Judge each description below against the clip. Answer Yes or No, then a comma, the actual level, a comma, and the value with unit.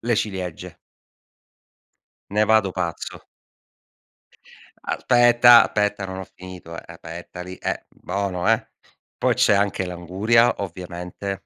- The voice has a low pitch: Yes, very low, 95 Hz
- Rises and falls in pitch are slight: No, average, 3.4 semitones